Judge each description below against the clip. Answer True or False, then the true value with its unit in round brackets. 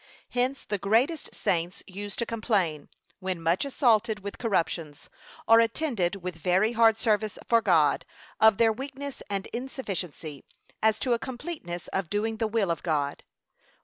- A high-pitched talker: True (210 Hz)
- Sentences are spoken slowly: False (150 wpm)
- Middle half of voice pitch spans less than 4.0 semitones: False (4.5 semitones)